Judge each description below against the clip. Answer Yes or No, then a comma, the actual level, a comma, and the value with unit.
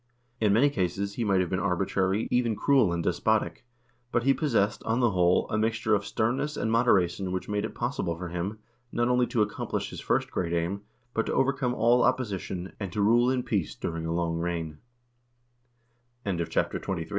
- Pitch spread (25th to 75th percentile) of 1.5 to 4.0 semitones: No, average, 4.8 semitones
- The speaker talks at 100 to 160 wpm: No, average, 170 wpm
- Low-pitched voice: Yes, low, 105 Hz